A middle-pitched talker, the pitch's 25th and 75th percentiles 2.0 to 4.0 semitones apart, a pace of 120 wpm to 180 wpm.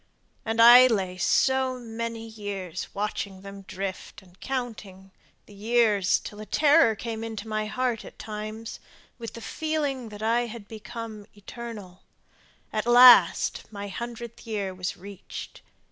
No: high, 220 Hz; average, 2.8 semitones; average, 140 wpm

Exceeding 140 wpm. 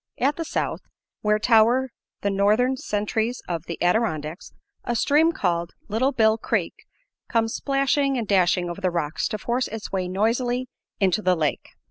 Yes: average, 160 wpm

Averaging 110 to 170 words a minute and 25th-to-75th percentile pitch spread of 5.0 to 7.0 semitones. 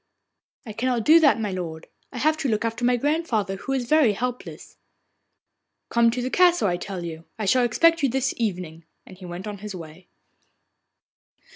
No: average, 185 wpm; wide, 5.6 semitones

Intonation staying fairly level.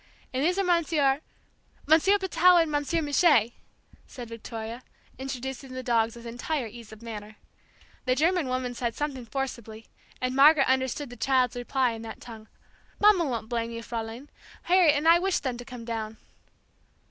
No: average, 4.4 semitones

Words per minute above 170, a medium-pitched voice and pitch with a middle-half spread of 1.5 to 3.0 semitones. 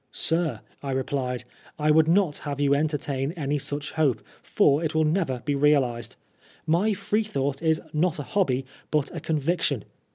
Yes: average, 180 wpm; medium, 150 Hz; average, 2.7 semitones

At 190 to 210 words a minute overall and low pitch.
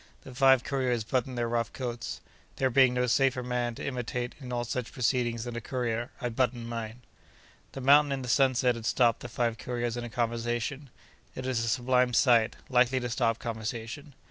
Yes: average, 195 wpm; low, 125 Hz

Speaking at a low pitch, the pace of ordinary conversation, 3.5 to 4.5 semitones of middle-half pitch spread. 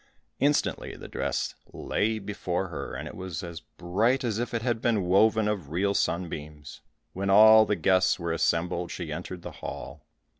Yes: very low, 95 Hz; average, 175 wpm; average, 4.1 semitones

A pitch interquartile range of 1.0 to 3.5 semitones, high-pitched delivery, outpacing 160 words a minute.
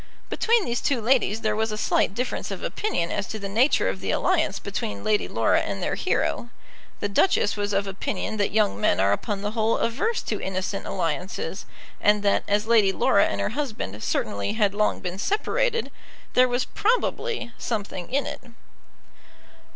No: average, 4.2 semitones; high, 210 Hz; average, 180 wpm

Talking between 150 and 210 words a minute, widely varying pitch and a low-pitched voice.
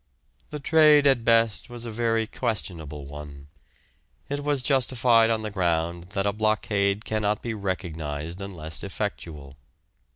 No: slow, 135 wpm; wide, 5.8 semitones; low, 105 Hz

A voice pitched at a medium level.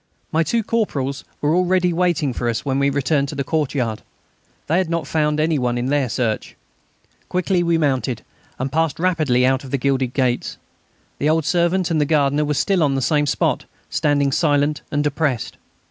Yes: medium, 145 Hz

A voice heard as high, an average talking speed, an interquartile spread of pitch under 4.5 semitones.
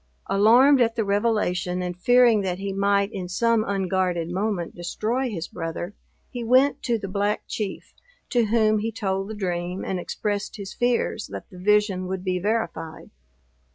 Yes: high, 200 Hz; average, 165 wpm; average, 3.5 semitones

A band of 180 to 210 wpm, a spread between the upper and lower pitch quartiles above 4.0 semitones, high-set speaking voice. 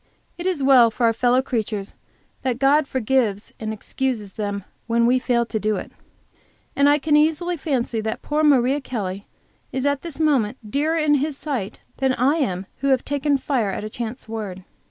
Yes: average, 190 wpm; average, 4.5 semitones; very high, 255 Hz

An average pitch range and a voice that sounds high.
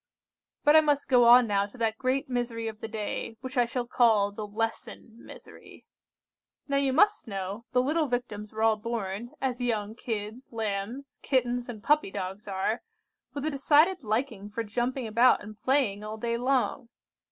Yes: average, 3.4 semitones; high, 235 Hz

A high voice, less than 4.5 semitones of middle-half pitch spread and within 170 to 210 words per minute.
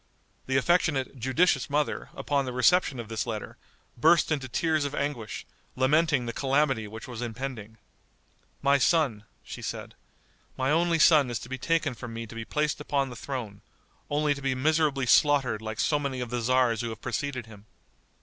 No: low, 130 Hz; average, 4.0 semitones; average, 180 wpm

